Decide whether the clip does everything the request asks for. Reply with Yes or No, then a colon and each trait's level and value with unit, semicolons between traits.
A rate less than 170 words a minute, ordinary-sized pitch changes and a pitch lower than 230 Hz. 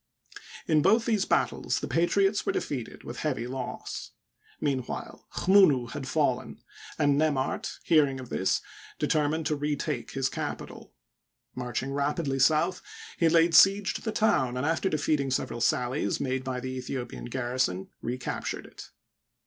Yes: average, 145 wpm; average, 4.0 semitones; medium, 140 Hz